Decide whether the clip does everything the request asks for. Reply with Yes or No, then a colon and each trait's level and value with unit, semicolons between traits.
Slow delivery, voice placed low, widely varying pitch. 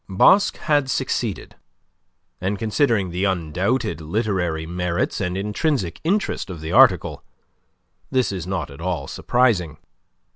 Yes: slow, 120 wpm; very low, 95 Hz; wide, 5.7 semitones